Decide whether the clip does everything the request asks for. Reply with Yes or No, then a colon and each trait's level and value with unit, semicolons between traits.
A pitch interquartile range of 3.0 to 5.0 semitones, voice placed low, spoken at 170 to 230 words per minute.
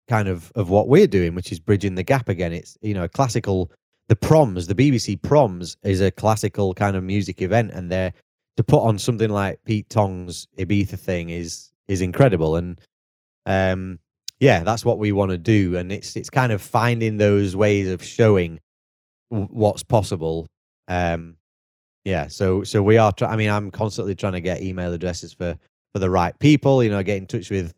Yes: average, 3.5 semitones; low, 100 Hz; average, 200 wpm